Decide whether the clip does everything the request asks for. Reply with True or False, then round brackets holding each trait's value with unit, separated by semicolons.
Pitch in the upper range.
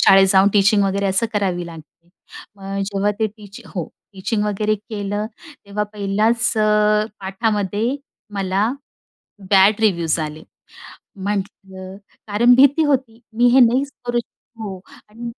True (205 Hz)